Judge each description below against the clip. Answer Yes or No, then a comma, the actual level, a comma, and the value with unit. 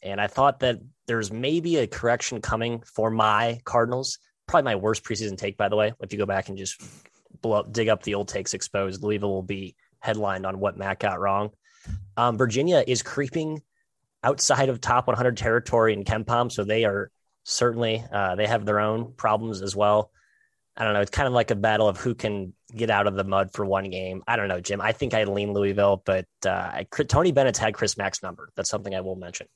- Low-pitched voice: Yes, low, 110 Hz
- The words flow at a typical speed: No, fast, 220 wpm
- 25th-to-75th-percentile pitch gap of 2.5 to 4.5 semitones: Yes, average, 3.0 semitones